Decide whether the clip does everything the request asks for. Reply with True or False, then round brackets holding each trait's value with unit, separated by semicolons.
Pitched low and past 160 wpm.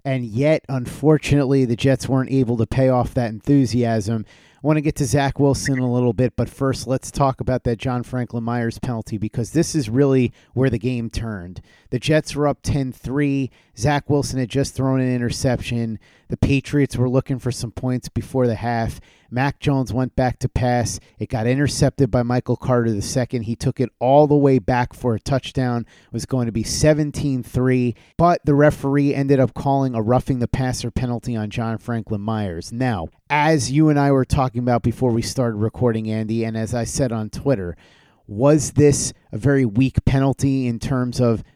True (125 Hz; 200 wpm)